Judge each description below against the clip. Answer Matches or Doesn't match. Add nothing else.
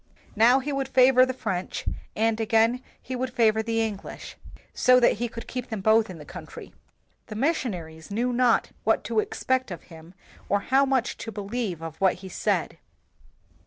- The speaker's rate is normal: Matches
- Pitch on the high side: Matches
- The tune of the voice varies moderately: Matches